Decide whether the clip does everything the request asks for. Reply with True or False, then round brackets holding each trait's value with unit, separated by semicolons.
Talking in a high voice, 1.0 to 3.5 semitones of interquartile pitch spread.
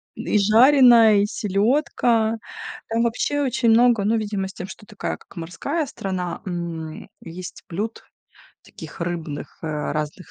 False (205 Hz; 4.8 semitones)